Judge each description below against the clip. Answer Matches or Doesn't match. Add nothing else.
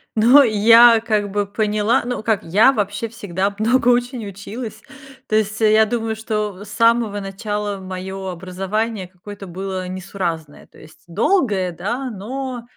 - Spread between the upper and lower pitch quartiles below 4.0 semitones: Matches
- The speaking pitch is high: Matches